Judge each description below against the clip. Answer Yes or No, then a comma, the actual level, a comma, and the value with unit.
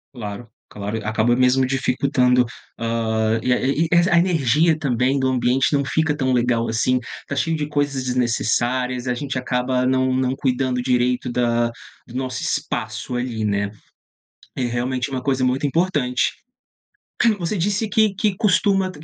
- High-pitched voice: No, low, 130 Hz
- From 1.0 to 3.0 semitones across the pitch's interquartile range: Yes, narrow, 2.6 semitones